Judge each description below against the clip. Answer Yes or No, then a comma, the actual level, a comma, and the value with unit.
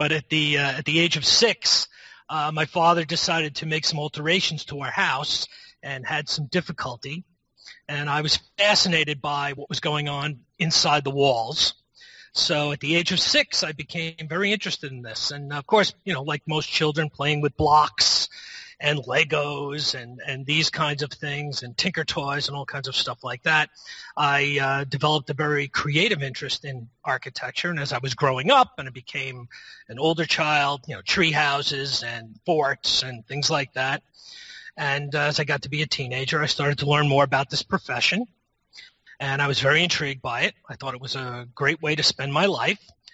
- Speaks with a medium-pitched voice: Yes, medium, 145 Hz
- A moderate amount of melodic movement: No, narrow, 2.2 semitones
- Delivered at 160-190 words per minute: No, average, 200 wpm